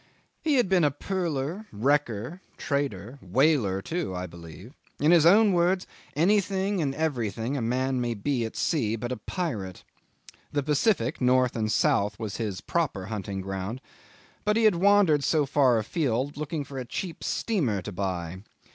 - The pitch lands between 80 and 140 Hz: Yes, low, 135 Hz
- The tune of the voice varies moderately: No, wide, 7.8 semitones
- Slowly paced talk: No, average, 160 wpm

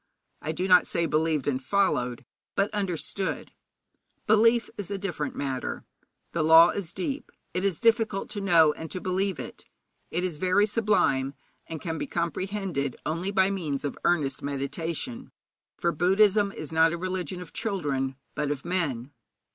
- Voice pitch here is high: No, medium, 175 Hz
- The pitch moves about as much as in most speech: Yes, average, 4.7 semitones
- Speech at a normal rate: Yes, average, 160 wpm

